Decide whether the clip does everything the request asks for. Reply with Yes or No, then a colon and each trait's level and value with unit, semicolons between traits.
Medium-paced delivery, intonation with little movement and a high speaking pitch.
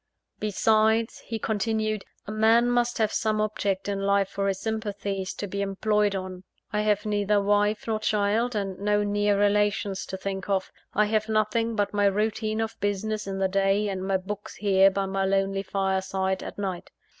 Yes: average, 180 wpm; narrow, 1.7 semitones; high, 205 Hz